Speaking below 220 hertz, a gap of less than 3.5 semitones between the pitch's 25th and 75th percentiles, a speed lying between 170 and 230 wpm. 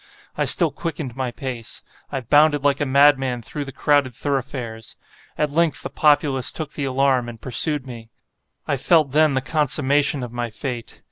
Yes: low, 135 Hz; average, 2.8 semitones; average, 175 wpm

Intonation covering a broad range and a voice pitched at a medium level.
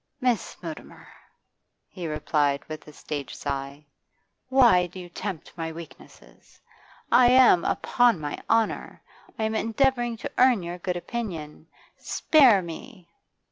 Yes: wide, 7.0 semitones; medium, 180 Hz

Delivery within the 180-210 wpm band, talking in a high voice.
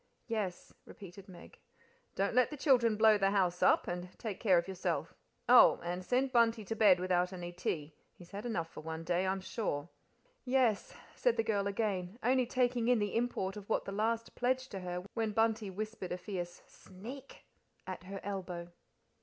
Yes: average, 185 wpm; high, 200 Hz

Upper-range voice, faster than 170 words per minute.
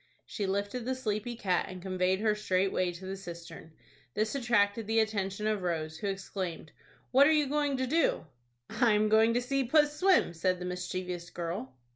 Yes: high, 205 Hz; average, 185 wpm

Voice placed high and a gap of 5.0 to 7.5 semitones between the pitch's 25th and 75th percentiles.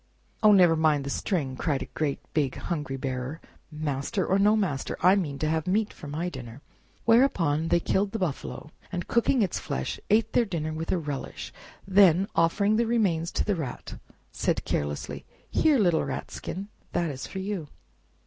No: medium, 165 Hz; average, 5.3 semitones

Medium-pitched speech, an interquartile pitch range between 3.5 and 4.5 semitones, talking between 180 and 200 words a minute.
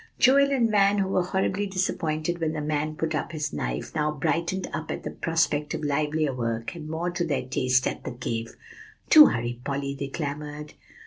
Yes: medium, 155 Hz; average, 4.0 semitones; average, 195 wpm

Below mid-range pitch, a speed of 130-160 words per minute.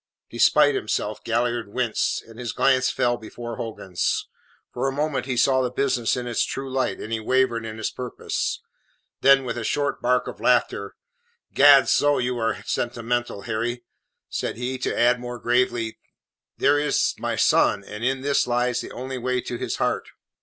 No: low, 125 Hz; average, 175 wpm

